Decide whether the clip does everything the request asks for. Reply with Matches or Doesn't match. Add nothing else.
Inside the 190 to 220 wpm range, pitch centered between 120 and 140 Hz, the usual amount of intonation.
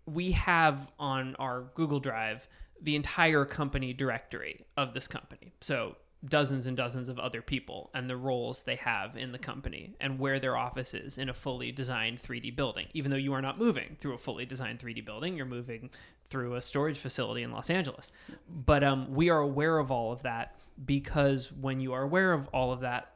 Doesn't match